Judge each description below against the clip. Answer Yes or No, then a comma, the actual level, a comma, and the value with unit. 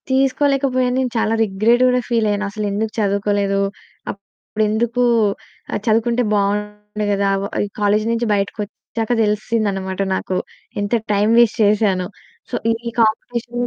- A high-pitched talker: Yes, high, 215 Hz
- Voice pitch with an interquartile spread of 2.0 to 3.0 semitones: Yes, narrow, 2.6 semitones